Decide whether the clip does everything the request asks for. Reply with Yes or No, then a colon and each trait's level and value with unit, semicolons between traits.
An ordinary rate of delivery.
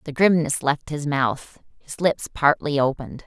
Yes: average, 165 wpm